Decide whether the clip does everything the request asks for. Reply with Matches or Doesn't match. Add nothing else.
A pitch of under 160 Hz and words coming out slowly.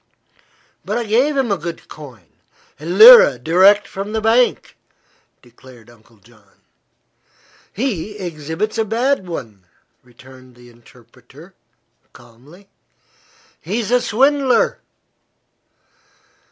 Doesn't match